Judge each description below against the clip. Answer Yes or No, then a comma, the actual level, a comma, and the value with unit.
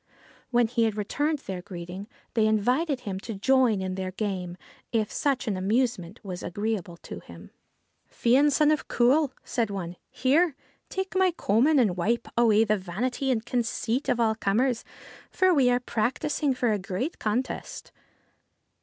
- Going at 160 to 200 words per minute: Yes, average, 170 wpm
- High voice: Yes, high, 230 Hz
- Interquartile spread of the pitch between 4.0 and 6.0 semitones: Yes, average, 4.7 semitones